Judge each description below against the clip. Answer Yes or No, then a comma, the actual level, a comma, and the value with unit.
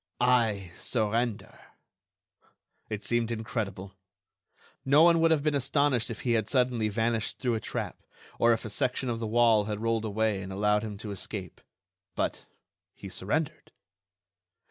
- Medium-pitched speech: No, low, 115 Hz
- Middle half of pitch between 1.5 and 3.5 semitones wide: Yes, average, 2.9 semitones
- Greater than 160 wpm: No, average, 150 wpm